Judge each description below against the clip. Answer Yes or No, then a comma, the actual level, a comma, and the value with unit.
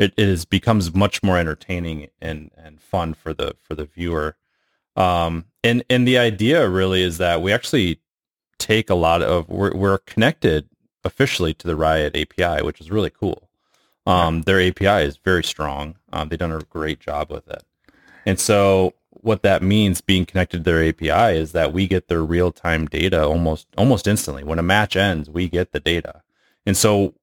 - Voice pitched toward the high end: No, very low, 90 Hz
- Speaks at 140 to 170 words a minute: No, average, 185 wpm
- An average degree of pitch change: Yes, average, 3.5 semitones